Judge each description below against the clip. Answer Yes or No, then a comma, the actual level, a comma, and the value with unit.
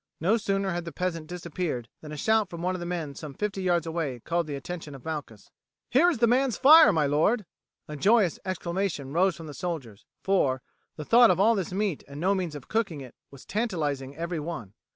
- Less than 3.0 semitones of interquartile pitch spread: No, average, 4.8 semitones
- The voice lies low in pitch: No, medium, 170 Hz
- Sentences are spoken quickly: Yes, fast, 215 wpm